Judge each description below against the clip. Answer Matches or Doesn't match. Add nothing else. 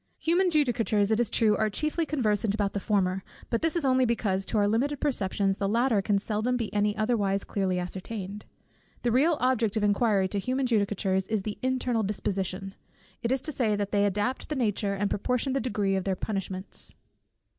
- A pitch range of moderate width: Matches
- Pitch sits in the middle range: Doesn't match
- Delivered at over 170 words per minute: Matches